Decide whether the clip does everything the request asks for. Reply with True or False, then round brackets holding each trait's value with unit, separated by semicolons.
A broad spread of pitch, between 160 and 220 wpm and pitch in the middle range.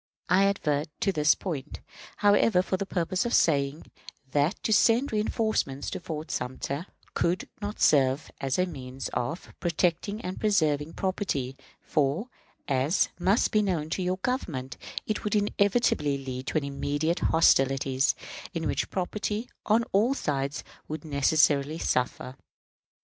False (6.0 semitones; 140 wpm; 160 Hz)